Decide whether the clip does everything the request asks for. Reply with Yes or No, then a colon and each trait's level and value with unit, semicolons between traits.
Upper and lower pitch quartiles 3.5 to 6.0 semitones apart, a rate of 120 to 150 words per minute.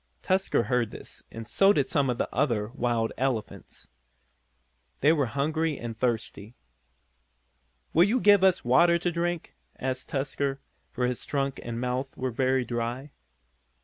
Yes: average, 4.6 semitones; average, 145 wpm